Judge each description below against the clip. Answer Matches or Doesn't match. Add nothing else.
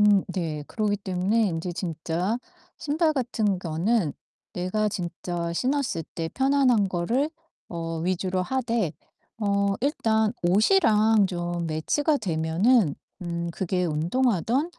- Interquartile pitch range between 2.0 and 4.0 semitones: Doesn't match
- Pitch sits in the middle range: Doesn't match